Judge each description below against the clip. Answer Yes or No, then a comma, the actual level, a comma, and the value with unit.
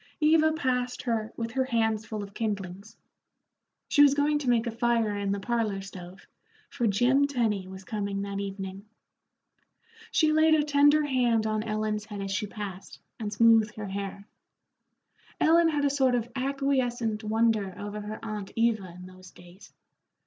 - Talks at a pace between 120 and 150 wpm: No, average, 165 wpm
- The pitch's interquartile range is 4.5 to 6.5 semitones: No, average, 4.1 semitones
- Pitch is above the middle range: Yes, high, 220 Hz